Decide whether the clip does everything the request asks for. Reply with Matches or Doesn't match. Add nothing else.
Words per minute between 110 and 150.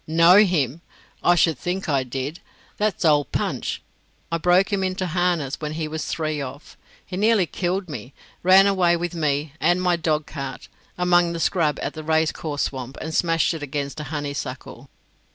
Doesn't match